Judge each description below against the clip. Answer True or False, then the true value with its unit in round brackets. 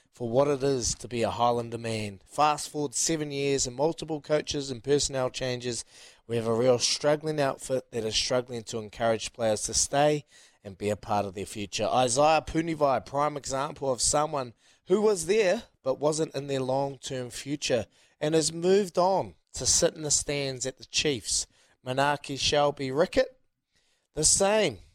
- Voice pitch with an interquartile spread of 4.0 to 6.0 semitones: True (4.3 semitones)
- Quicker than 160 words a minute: True (175 wpm)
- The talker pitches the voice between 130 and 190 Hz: True (135 Hz)